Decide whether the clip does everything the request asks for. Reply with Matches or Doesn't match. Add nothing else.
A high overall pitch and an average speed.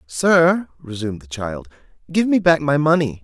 Doesn't match